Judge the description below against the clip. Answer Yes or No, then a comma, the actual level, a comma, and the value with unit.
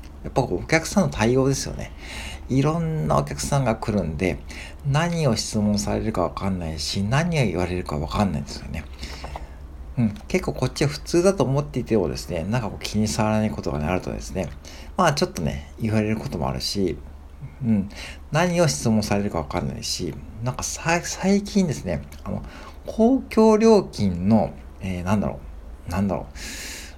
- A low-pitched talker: Yes, very low, 95 Hz